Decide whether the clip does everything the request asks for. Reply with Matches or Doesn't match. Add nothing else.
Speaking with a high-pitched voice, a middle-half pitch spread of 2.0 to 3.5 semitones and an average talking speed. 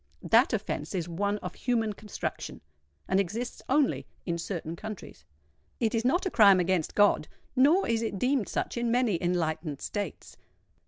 Doesn't match